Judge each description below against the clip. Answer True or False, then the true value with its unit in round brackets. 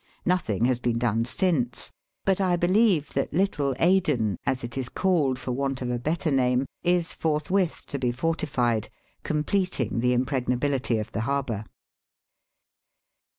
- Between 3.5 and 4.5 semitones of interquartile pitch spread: False (5.6 semitones)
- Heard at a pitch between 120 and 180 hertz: True (135 Hz)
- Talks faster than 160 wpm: False (145 wpm)